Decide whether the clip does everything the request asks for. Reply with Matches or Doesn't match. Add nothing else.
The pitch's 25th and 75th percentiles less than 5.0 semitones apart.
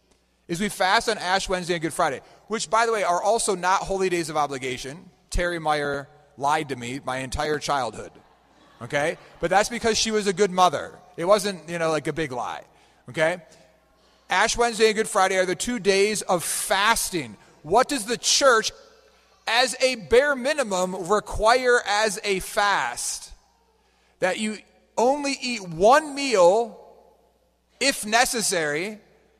Doesn't match